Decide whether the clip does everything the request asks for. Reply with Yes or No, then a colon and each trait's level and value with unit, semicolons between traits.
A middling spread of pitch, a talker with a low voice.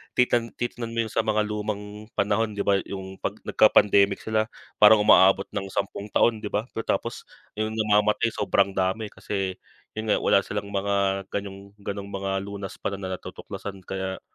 No: narrow, 1.6 semitones; low, 100 Hz